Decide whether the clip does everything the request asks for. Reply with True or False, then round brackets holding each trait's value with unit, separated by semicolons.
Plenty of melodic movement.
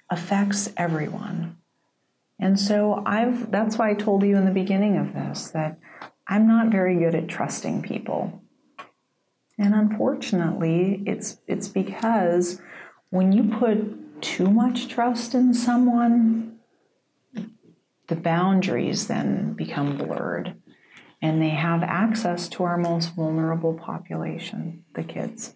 False (4.3 semitones)